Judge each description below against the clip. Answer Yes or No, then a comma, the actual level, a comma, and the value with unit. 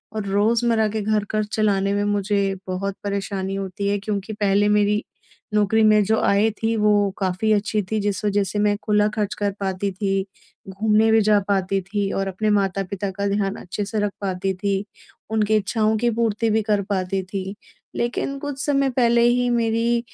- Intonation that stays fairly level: Yes, narrow, 1.7 semitones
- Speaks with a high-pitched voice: Yes, high, 205 Hz